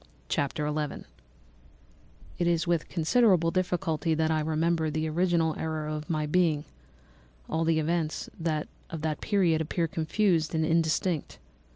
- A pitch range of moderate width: No, narrow, 1.7 semitones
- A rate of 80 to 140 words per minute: Yes, slow, 135 wpm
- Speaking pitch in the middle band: Yes, medium, 160 Hz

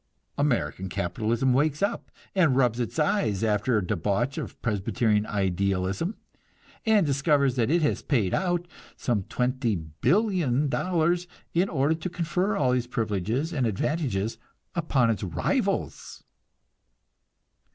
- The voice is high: No, low, 125 Hz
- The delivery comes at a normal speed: No, slow, 120 wpm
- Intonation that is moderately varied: No, wide, 7.3 semitones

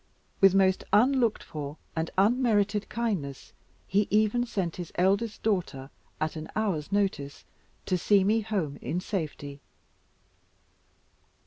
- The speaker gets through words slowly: Yes, slow, 120 wpm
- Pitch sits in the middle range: No, high, 195 Hz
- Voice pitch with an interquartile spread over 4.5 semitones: Yes, average, 5.0 semitones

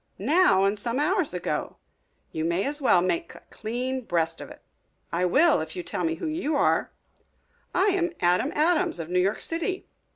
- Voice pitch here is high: Yes, high, 240 Hz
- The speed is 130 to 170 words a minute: No, average, 195 wpm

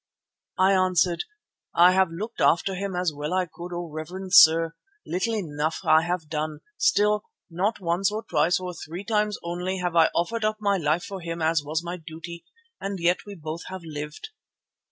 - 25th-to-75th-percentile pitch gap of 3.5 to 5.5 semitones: No, average, 2.8 semitones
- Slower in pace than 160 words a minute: No, average, 190 wpm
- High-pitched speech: No, medium, 175 Hz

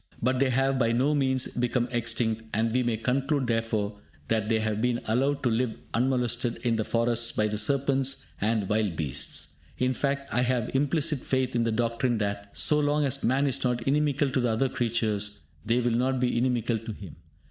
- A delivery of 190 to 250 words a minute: Yes, average, 200 wpm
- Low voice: Yes, low, 120 Hz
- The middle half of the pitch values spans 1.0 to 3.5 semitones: Yes, average, 2.8 semitones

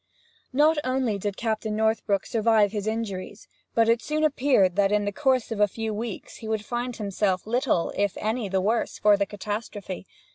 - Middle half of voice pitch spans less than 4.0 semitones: Yes, narrow, 2.5 semitones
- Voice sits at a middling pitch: No, high, 220 Hz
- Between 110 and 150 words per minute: No, average, 185 wpm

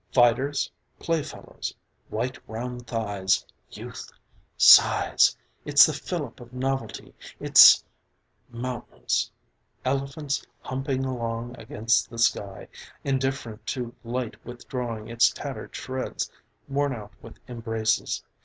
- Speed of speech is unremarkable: No, slow, 100 wpm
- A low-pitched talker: Yes, low, 120 Hz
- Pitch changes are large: No, narrow, 2.6 semitones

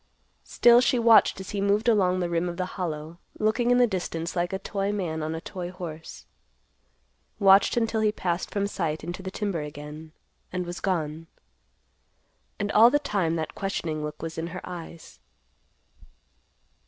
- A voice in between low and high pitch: Yes, medium, 180 Hz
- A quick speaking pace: No, average, 170 wpm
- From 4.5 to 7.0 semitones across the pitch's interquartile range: No, average, 3.8 semitones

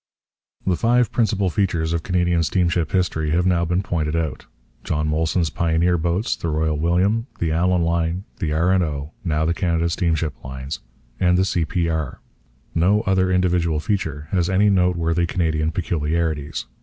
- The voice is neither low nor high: No, very low, 85 Hz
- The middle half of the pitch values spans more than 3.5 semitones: No, narrow, 2.4 semitones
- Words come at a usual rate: Yes, average, 155 wpm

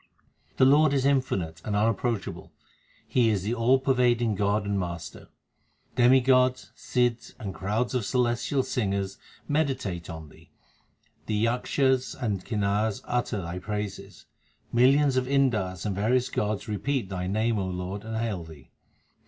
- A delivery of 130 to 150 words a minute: Yes, average, 140 wpm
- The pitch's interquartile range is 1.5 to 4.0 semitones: No, average, 4.5 semitones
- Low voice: Yes, low, 110 Hz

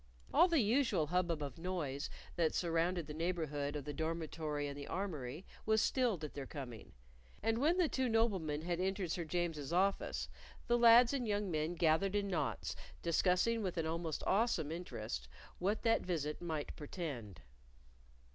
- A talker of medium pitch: Yes, medium, 170 Hz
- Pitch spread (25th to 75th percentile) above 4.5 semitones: Yes, average, 4.9 semitones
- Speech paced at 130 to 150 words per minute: No, average, 165 wpm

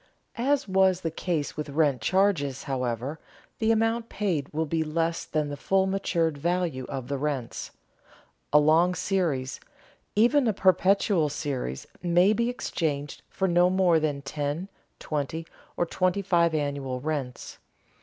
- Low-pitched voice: No, medium, 160 Hz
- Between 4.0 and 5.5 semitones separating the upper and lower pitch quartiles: Yes, average, 4.9 semitones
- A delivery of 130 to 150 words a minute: Yes, average, 145 wpm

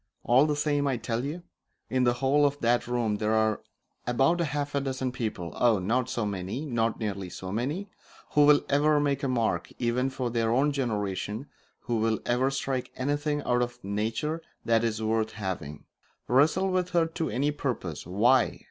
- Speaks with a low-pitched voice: Yes, low, 125 Hz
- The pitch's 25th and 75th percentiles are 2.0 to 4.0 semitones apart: No, average, 4.5 semitones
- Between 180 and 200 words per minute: Yes, average, 185 wpm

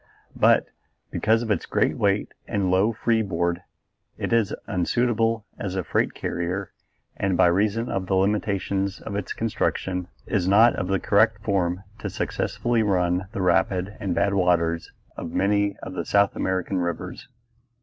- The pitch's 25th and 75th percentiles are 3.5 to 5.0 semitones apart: No, narrow, 2.4 semitones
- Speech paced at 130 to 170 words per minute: Yes, average, 160 wpm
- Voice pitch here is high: No, low, 100 Hz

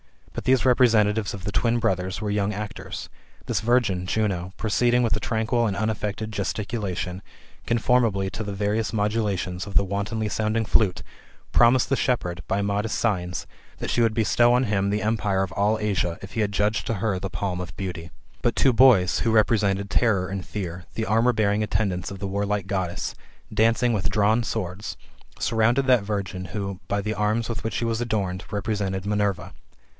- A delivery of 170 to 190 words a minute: Yes, average, 180 wpm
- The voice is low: Yes, low, 105 Hz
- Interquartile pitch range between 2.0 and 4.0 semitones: Yes, narrow, 2.5 semitones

